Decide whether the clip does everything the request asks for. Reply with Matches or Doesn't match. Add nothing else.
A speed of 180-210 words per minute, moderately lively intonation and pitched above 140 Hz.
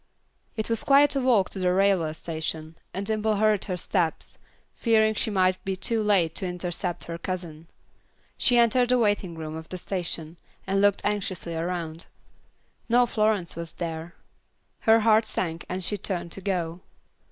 Doesn't match